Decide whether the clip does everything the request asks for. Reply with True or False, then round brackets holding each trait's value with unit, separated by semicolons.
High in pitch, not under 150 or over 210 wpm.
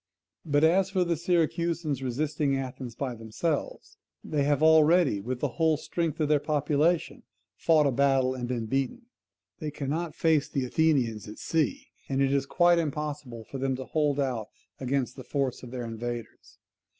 False (140 Hz; 170 wpm)